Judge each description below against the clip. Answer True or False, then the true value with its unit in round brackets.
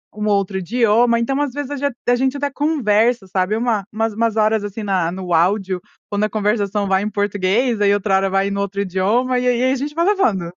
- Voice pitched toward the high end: True (210 Hz)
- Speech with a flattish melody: False (4.0 semitones)